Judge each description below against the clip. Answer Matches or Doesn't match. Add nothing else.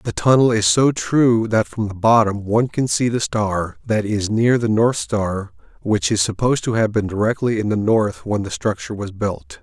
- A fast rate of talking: Matches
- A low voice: Matches